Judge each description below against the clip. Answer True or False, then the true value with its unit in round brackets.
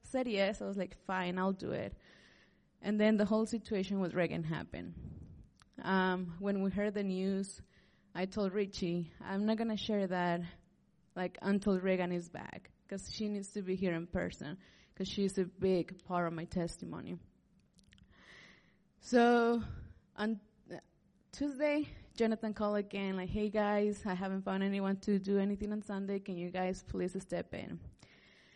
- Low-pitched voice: False (195 Hz)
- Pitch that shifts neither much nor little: False (2.2 semitones)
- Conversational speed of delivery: True (160 wpm)